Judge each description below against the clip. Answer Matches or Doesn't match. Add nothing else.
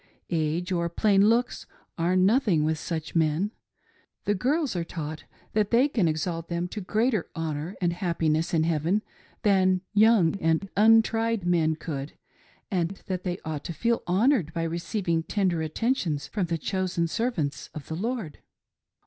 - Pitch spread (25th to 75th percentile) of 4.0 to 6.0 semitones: Matches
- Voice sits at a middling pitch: Matches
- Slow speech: Doesn't match